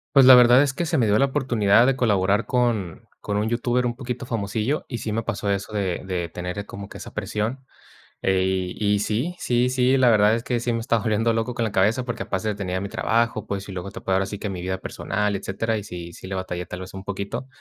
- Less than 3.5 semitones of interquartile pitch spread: No, average, 3.8 semitones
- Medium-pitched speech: No, low, 110 Hz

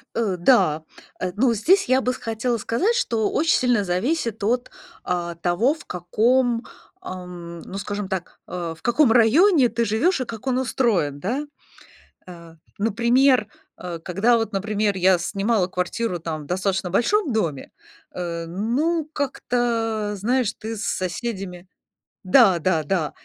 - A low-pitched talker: No, high, 215 Hz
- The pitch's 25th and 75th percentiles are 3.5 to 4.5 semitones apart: No, average, 5.3 semitones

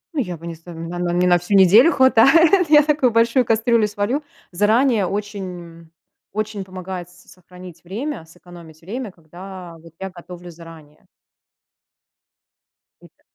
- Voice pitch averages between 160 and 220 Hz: Yes, medium, 185 Hz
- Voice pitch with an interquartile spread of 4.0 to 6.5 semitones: Yes, average, 4.7 semitones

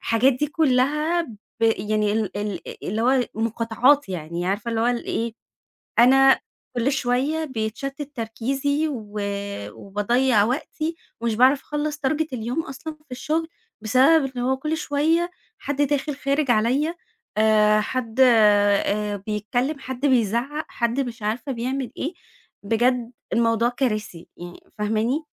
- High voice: Yes, high, 245 Hz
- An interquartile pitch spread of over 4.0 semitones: Yes, average, 4.4 semitones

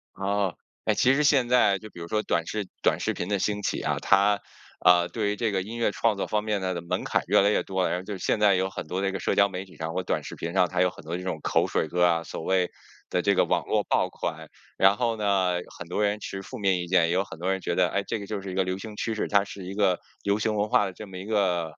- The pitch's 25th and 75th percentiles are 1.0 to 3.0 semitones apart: Yes, narrow, 2.5 semitones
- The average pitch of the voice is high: No, very low, 95 Hz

